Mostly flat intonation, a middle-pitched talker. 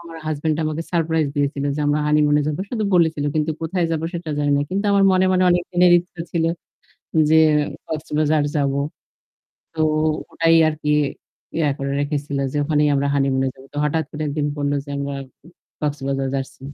Yes: narrow, 2.3 semitones; medium, 150 Hz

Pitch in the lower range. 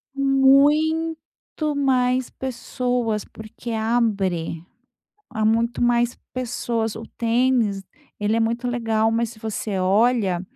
No: high, 235 Hz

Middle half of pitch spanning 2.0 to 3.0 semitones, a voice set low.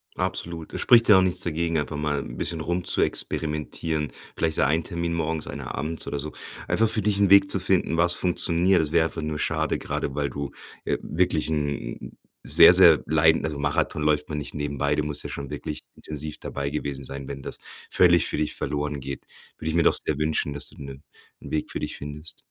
Yes: average, 2.7 semitones; very low, 75 Hz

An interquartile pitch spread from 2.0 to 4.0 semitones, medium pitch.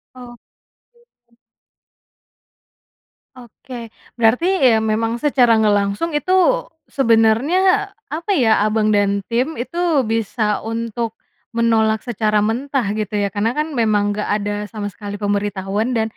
No: average, 3.3 semitones; high, 225 Hz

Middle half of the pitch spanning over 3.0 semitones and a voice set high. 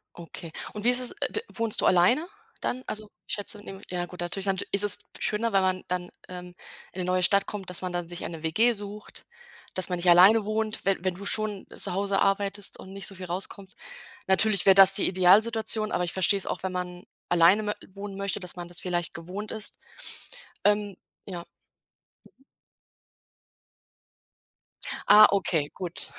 No: narrow, 2.6 semitones; high, 195 Hz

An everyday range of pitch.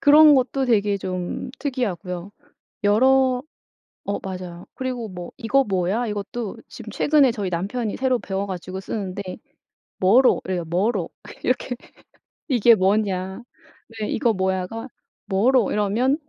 Yes: average, 4.9 semitones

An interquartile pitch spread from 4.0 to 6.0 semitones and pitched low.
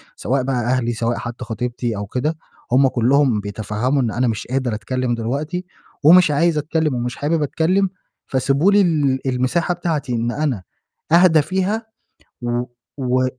Yes: average, 4.8 semitones; low, 130 Hz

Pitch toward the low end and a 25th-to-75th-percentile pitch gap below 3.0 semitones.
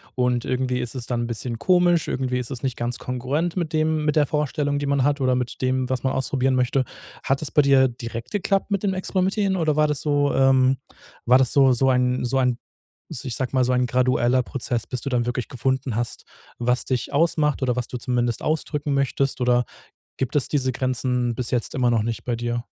Yes: low, 130 Hz; narrow, 2.6 semitones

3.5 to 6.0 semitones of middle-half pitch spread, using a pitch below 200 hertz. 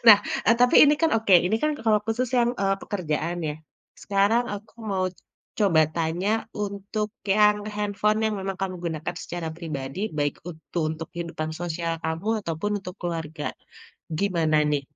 Yes: average, 4.5 semitones; medium, 185 Hz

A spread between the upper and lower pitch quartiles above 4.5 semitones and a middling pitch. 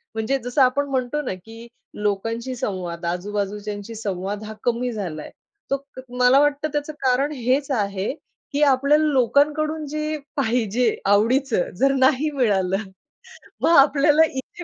No: average, 5.2 semitones; very high, 250 Hz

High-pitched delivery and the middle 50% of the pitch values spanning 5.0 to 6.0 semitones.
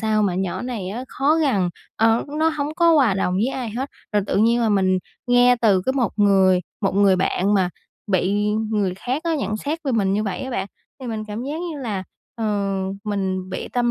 No: high, 215 Hz; average, 4.4 semitones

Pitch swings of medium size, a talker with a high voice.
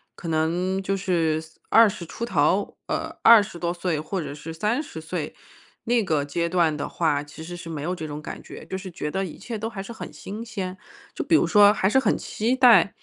No: average, 4.6 semitones; medium, 180 Hz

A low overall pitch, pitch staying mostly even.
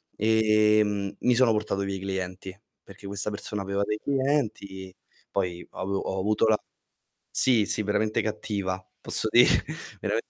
Yes: low, 105 Hz; narrow, 1.8 semitones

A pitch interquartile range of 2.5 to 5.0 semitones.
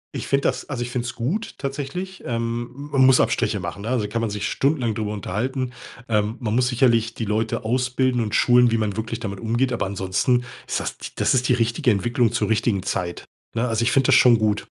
Yes: average, 2.9 semitones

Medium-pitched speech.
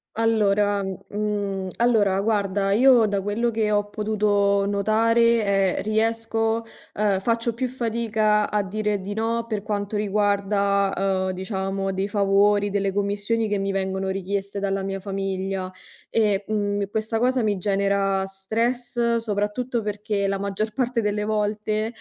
No: high, 205 Hz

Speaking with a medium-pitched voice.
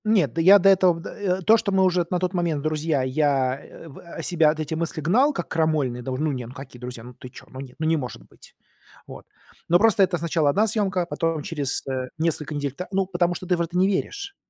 Yes: medium, 165 Hz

